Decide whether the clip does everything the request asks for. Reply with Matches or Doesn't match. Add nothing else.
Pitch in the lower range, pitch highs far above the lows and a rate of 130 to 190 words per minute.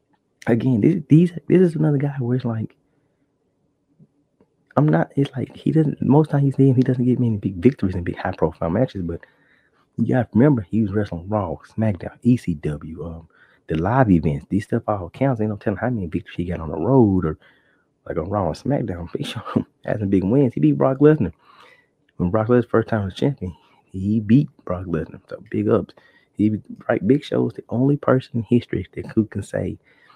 Doesn't match